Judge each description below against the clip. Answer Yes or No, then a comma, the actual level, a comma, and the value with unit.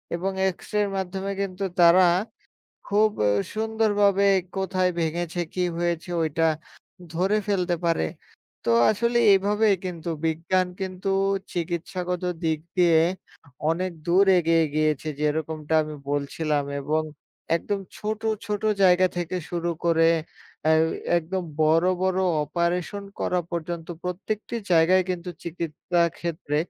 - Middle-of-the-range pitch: Yes, medium, 175 Hz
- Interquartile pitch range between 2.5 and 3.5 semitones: Yes, average, 2.8 semitones